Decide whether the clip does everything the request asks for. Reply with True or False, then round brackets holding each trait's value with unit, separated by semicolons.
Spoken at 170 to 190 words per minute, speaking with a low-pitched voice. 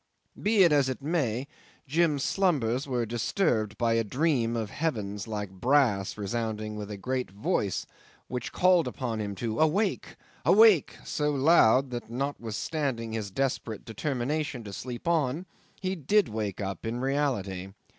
False (145 wpm; 125 Hz)